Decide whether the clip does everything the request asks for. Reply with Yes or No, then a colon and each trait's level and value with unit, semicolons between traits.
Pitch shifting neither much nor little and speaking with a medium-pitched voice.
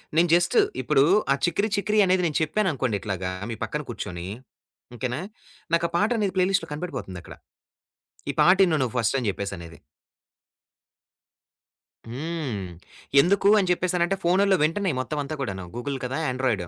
No: wide, 7.3 semitones; medium, 155 Hz